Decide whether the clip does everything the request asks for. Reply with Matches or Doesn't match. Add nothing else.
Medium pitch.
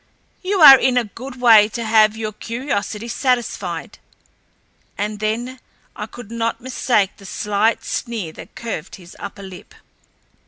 Doesn't match